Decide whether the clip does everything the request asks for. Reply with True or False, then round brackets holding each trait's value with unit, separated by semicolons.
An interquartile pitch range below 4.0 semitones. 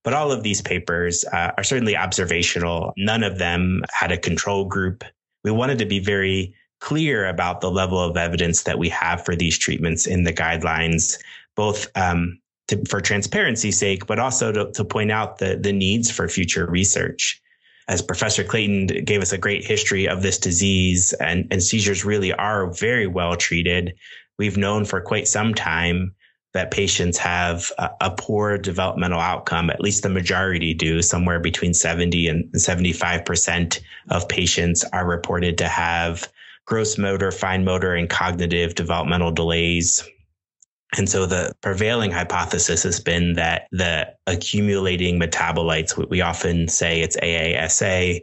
True (2.7 semitones)